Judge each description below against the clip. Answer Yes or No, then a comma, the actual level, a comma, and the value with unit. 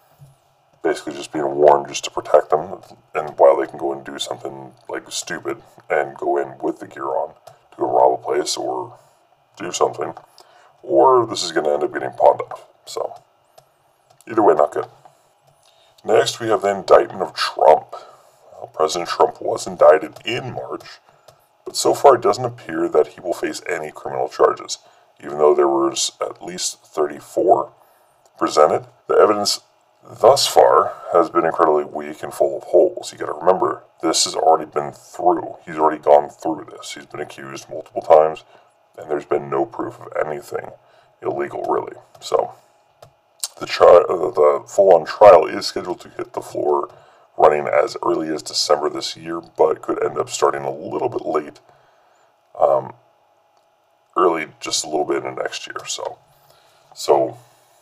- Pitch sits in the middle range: No, very low, 75 Hz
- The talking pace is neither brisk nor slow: Yes, average, 170 wpm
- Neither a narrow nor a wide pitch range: Yes, average, 3.2 semitones